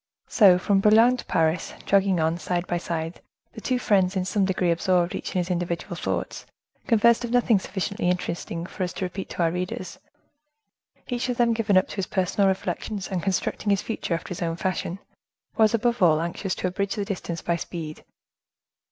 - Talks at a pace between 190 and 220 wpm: Yes, average, 195 wpm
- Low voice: No, medium, 185 Hz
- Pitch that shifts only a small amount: No, average, 3.0 semitones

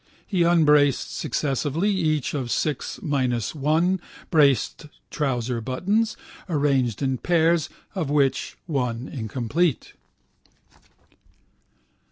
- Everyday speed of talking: No, slow, 90 wpm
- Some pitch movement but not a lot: Yes, average, 4.3 semitones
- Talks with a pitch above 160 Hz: No, medium, 145 Hz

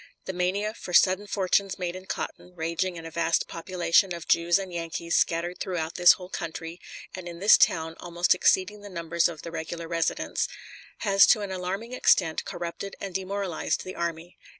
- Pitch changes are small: Yes, narrow, 2.1 semitones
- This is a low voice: No, medium, 175 Hz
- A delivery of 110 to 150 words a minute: No, average, 180 wpm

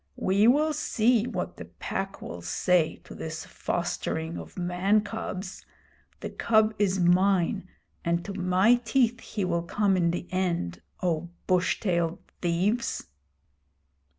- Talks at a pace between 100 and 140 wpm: Yes, slow, 135 wpm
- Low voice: No, medium, 185 Hz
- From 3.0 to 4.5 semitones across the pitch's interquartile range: Yes, average, 3.7 semitones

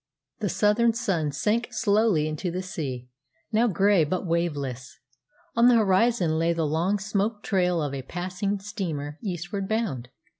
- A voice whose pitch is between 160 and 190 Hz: Yes, medium, 185 Hz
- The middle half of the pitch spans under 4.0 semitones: No, average, 4.9 semitones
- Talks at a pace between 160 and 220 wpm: No, average, 150 wpm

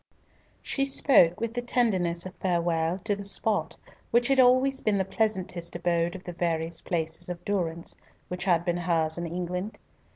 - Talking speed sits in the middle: Yes, average, 170 wpm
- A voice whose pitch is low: No, medium, 180 Hz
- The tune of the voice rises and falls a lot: No, average, 4.2 semitones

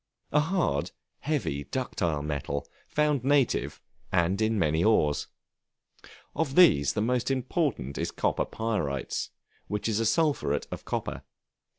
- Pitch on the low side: Yes, low, 110 Hz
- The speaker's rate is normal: No, slow, 125 wpm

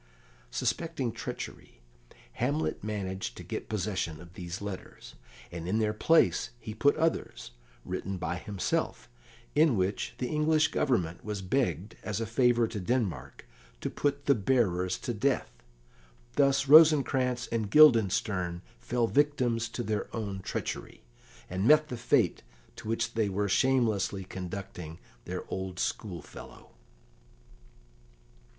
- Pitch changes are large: Yes, wide, 5.7 semitones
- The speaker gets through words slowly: Yes, slow, 130 wpm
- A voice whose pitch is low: Yes, low, 110 Hz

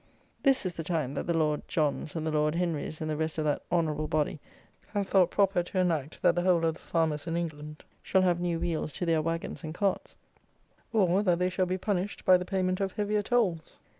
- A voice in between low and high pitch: Yes, medium, 170 Hz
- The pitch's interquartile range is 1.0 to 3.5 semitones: Yes, average, 2.9 semitones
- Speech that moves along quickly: Yes, fast, 225 wpm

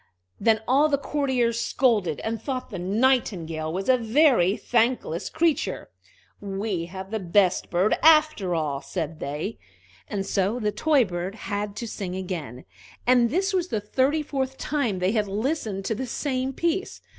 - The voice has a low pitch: No, high, 220 Hz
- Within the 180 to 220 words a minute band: No, average, 160 wpm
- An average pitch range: No, wide, 5.9 semitones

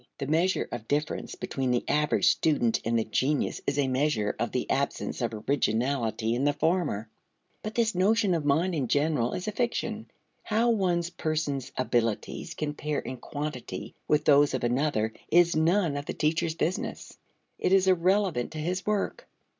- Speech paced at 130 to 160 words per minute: No, average, 170 wpm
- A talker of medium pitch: Yes, medium, 150 Hz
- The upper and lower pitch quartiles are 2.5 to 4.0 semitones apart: No, wide, 5.5 semitones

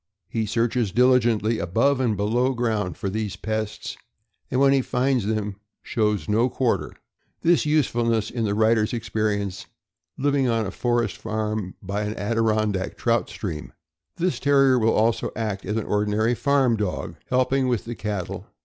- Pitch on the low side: Yes, low, 110 Hz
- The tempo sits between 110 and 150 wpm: No, average, 160 wpm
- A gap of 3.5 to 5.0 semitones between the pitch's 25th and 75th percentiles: No, average, 2.9 semitones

